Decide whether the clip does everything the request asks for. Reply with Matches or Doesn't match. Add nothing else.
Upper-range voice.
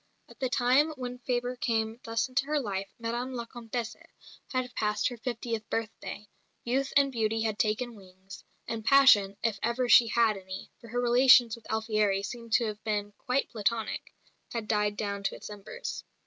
Matches